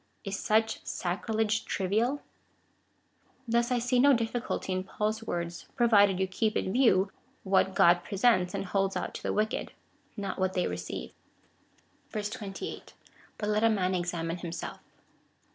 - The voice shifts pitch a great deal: No, average, 3.2 semitones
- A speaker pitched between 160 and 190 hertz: No, high, 200 Hz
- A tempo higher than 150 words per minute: No, average, 145 wpm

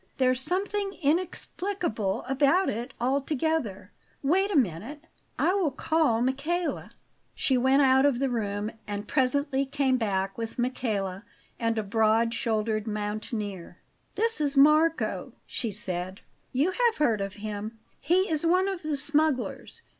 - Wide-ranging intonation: Yes, wide, 6.3 semitones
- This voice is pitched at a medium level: No, very high, 260 Hz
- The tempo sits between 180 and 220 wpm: No, average, 140 wpm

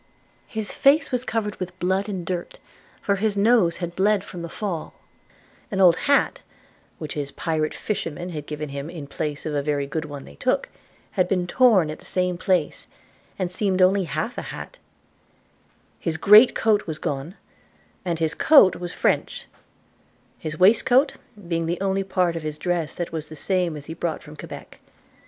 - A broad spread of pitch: No, average, 3.9 semitones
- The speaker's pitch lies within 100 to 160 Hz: No, medium, 175 Hz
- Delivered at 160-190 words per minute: Yes, average, 180 wpm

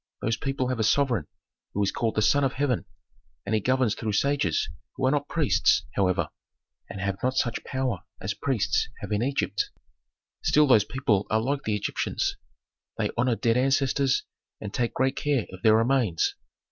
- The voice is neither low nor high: No, low, 120 Hz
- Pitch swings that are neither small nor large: Yes, average, 4.3 semitones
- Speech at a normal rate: Yes, average, 180 wpm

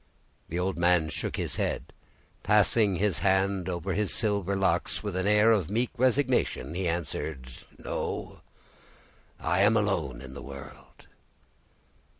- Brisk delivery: No, average, 145 wpm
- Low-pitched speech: Yes, very low, 95 Hz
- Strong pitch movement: No, average, 3.9 semitones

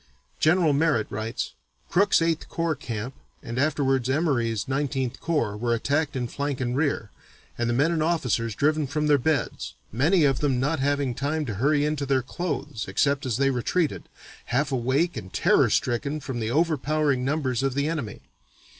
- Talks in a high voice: No, medium, 140 Hz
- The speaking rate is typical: Yes, average, 170 wpm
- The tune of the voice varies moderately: Yes, average, 3.8 semitones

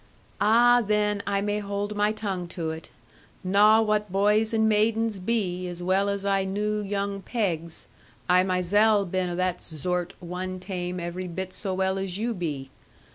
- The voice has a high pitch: Yes, high, 195 Hz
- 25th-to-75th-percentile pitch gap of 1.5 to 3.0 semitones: Yes, narrow, 2.6 semitones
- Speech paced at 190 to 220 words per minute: No, average, 170 wpm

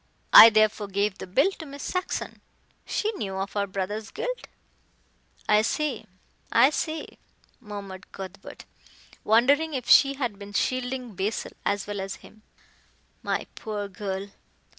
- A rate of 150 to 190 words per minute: No, average, 140 wpm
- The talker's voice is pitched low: No, high, 215 Hz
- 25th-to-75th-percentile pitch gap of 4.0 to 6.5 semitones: Yes, average, 5.3 semitones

